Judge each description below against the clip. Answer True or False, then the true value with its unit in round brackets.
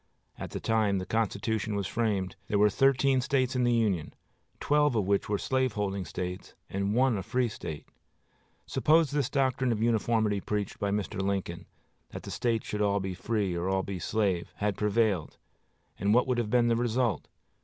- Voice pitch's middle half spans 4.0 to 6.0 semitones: False (3.6 semitones)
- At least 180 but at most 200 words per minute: True (185 wpm)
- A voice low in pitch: True (105 Hz)